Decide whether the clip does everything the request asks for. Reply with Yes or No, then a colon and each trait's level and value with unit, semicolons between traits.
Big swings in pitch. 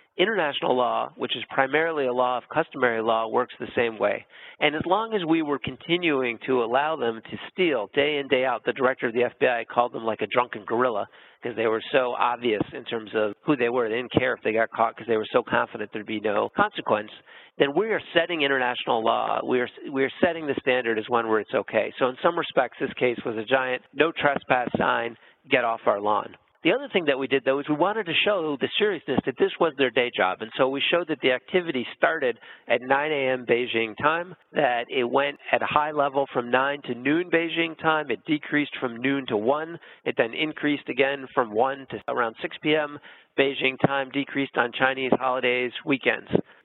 No: average, 3.9 semitones